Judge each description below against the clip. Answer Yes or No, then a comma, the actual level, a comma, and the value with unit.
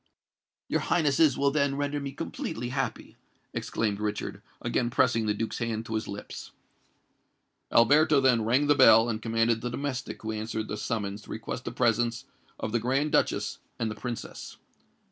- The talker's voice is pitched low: Yes, low, 120 Hz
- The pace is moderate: Yes, average, 165 wpm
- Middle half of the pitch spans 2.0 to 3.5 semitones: No, average, 3.9 semitones